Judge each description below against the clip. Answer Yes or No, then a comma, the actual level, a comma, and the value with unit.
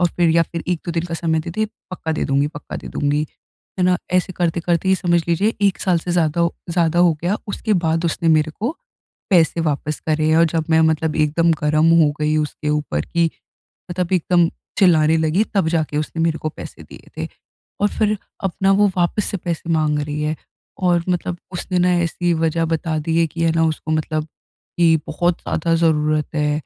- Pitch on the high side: No, medium, 165 Hz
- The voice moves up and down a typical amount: No, narrow, 2.1 semitones